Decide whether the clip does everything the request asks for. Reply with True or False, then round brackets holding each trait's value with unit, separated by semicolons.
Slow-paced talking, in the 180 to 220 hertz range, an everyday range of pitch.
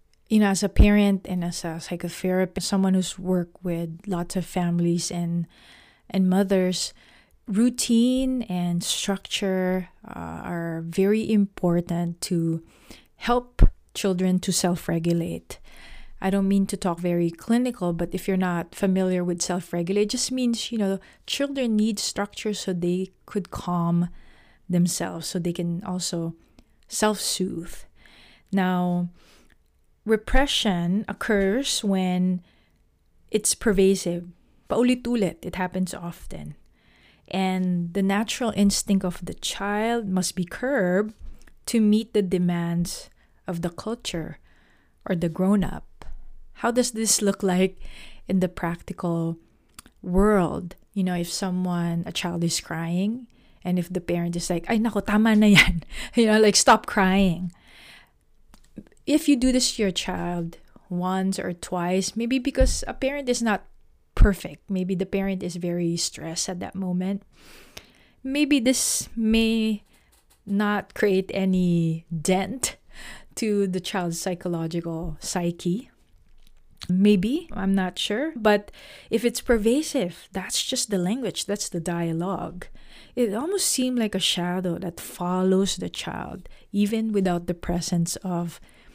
True (130 wpm; 185 Hz; 3.2 semitones)